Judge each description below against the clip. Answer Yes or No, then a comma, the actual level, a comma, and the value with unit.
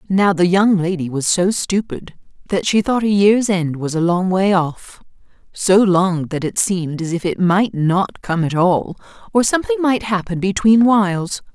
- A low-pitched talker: No, medium, 185 Hz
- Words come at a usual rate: Yes, average, 185 wpm